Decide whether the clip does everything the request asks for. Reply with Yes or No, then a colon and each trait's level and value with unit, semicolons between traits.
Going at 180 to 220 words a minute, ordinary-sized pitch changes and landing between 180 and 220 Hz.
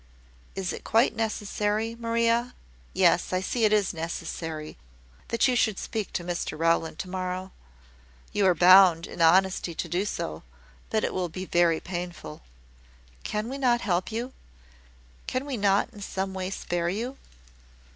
No: average, 155 wpm; average, 4.2 semitones; high, 190 Hz